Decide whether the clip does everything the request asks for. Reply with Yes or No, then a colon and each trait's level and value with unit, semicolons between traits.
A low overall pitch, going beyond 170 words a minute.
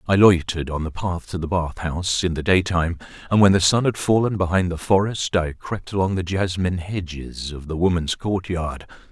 Yes: very low, 90 Hz; fast, 205 wpm